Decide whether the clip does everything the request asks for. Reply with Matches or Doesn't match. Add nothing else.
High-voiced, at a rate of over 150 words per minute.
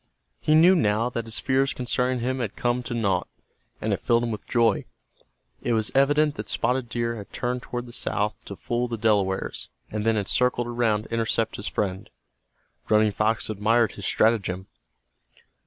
Doesn't match